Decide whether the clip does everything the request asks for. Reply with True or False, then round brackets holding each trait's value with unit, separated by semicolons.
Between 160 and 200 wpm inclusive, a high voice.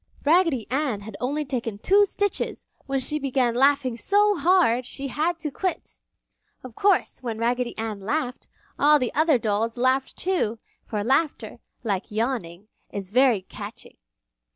False (150 wpm; 255 Hz)